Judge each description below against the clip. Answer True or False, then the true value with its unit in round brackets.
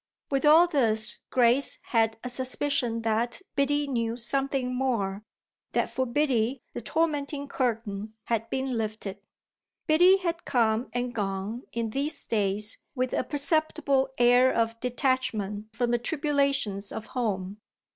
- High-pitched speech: True (245 Hz)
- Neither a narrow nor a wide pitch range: True (4.0 semitones)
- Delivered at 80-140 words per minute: True (135 wpm)